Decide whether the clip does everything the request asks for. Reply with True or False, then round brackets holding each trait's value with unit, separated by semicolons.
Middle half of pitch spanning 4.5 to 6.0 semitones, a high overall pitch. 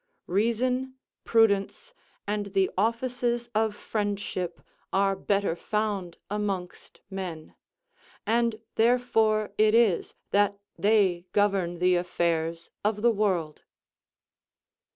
False (3.2 semitones; 205 Hz)